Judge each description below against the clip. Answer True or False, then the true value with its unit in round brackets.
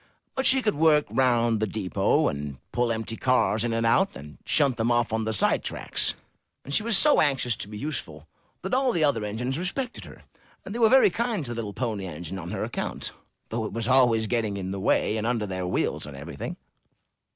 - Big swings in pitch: True (5.9 semitones)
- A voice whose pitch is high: False (115 Hz)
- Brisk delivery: True (220 wpm)